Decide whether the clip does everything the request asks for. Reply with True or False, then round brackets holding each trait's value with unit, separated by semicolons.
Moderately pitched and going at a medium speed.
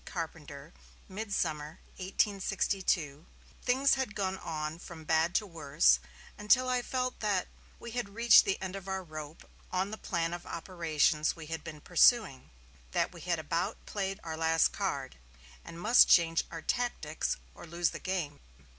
True (175 Hz; 155 wpm)